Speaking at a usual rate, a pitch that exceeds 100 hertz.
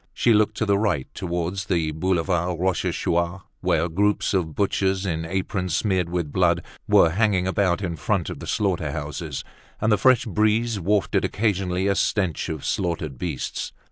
No: average, 165 wpm; very low, 95 Hz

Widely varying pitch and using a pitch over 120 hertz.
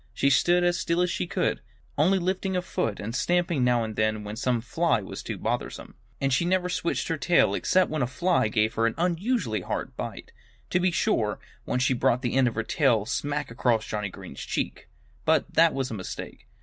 Yes: wide, 7.6 semitones; low, 135 Hz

